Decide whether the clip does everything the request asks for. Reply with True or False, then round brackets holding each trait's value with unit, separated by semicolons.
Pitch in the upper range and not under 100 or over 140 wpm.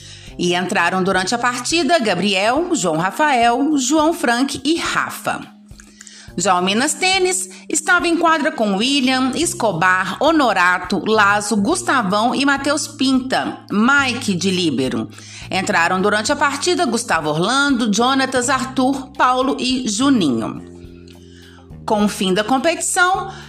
True (245 Hz; 120 wpm)